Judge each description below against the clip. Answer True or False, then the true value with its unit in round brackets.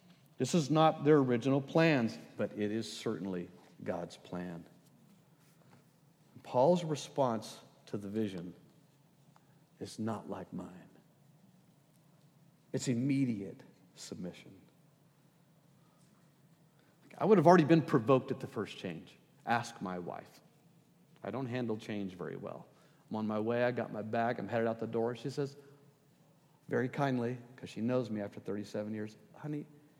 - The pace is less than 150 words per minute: True (140 wpm)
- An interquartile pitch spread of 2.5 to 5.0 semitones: False (5.6 semitones)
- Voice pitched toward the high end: False (140 Hz)